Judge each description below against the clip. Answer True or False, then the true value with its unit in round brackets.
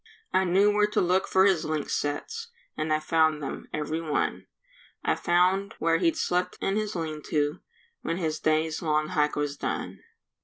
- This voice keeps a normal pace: True (180 wpm)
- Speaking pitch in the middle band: True (165 Hz)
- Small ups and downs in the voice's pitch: False (3.6 semitones)